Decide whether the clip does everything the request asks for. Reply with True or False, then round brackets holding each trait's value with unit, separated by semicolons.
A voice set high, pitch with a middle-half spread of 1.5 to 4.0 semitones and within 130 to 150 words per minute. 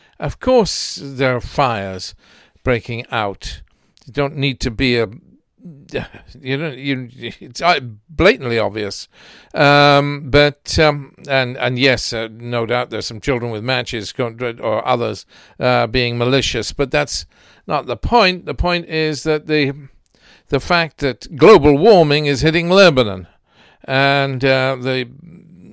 False (135 Hz; 3.5 semitones; 140 wpm)